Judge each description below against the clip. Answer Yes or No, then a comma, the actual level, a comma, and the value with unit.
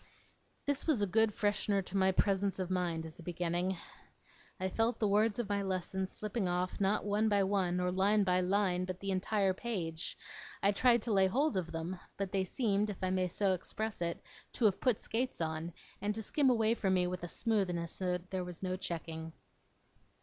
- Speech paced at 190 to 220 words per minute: Yes, fast, 205 wpm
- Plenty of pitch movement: No, average, 2.7 semitones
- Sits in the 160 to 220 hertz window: Yes, high, 190 Hz